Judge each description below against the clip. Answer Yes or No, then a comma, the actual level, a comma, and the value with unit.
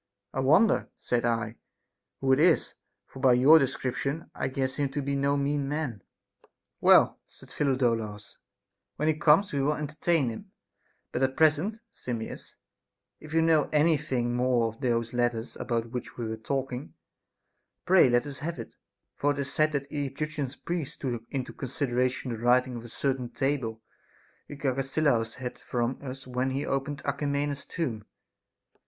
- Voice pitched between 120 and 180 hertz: Yes, low, 135 Hz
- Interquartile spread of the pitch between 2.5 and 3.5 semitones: Yes, average, 3.1 semitones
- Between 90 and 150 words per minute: No, average, 170 wpm